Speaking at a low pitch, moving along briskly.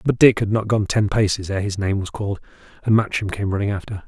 Yes: low, 105 Hz; fast, 250 wpm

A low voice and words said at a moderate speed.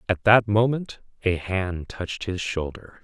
Yes: low, 100 Hz; average, 160 wpm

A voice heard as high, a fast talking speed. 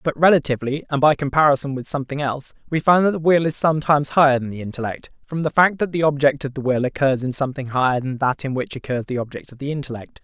No: medium, 140 Hz; fast, 245 wpm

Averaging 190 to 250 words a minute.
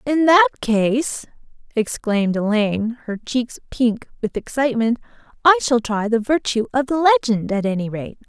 No: average, 150 wpm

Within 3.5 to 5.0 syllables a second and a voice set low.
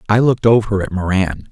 No: 6.1 syllables/s; low, 100 Hz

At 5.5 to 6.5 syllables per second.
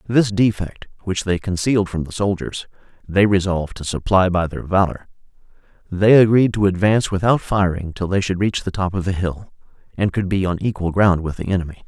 Yes: 5.6 syllables/s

